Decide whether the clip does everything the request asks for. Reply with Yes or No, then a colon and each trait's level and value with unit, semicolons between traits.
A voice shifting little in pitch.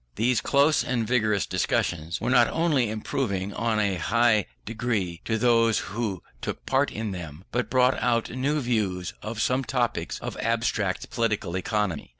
No: average, 3.8 semitones